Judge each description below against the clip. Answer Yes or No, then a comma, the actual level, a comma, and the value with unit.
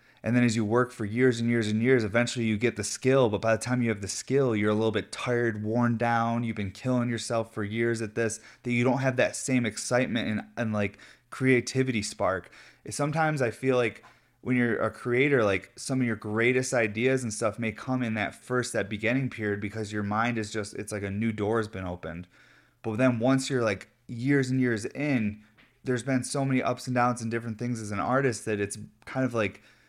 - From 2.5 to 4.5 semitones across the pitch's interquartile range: Yes, average, 2.8 semitones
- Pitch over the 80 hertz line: Yes, low, 115 Hz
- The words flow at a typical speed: No, fast, 230 wpm